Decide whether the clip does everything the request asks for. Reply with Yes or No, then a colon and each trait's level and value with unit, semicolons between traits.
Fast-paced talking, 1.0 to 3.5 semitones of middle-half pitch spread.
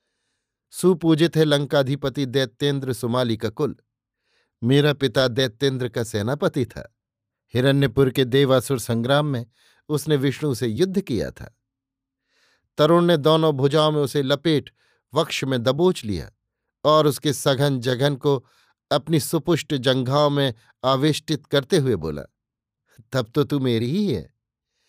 No: average, 130 wpm; narrow, 2.5 semitones